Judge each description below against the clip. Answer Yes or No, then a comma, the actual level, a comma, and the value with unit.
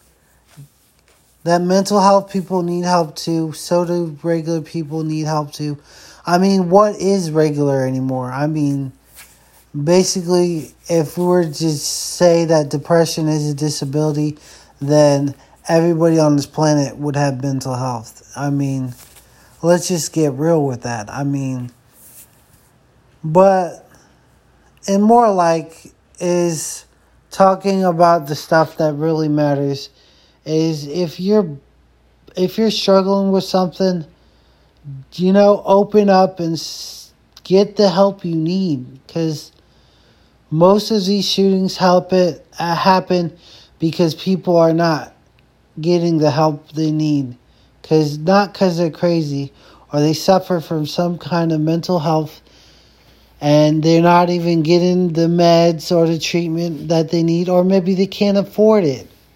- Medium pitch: Yes, medium, 165 Hz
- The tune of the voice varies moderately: Yes, average, 3.6 semitones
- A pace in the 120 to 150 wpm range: Yes, slow, 135 wpm